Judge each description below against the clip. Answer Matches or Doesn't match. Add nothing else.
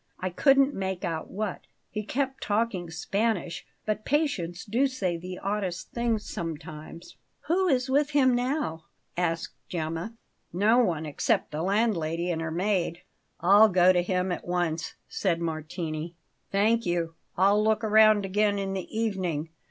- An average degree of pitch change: Matches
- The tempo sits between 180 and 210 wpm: Doesn't match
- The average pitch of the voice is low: Doesn't match